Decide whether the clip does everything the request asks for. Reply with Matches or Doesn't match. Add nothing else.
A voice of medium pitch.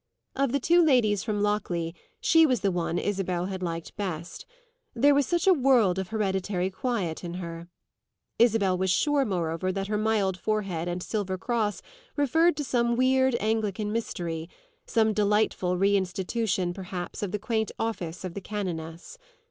Doesn't match